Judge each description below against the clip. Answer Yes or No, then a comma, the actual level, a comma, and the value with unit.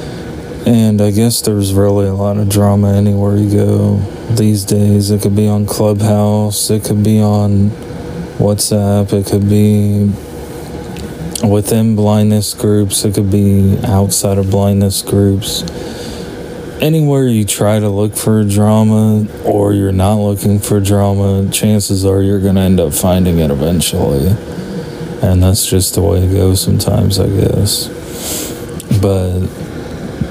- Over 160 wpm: No, average, 140 wpm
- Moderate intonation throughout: No, narrow, 1.2 semitones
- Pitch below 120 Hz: Yes, low, 100 Hz